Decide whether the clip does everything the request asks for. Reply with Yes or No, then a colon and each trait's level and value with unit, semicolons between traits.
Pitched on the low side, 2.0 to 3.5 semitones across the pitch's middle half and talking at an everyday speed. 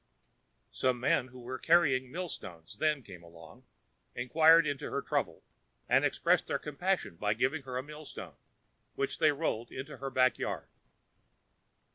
No: low, 130 Hz; average, 4.0 semitones; average, 155 wpm